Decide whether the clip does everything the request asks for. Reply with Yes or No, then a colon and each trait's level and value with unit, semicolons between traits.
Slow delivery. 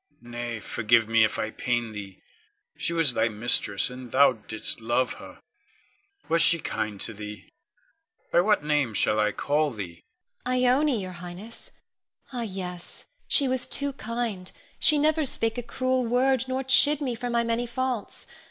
No: average, 165 wpm